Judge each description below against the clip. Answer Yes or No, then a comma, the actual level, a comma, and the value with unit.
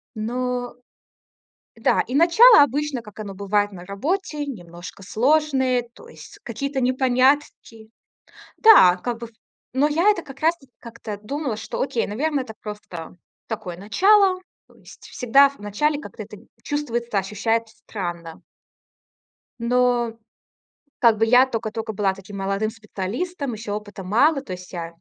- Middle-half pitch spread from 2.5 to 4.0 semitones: No, average, 5.3 semitones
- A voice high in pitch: Yes, high, 235 Hz